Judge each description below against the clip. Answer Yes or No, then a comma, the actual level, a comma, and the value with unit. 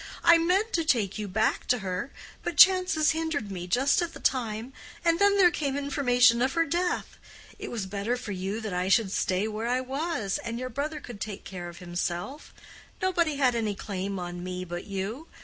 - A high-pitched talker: Yes, high, 240 Hz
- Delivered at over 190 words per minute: Yes, average, 200 wpm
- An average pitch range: No, wide, 7.8 semitones